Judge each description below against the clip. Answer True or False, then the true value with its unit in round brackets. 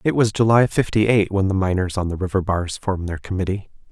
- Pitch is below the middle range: True (100 Hz)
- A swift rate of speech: True (230 wpm)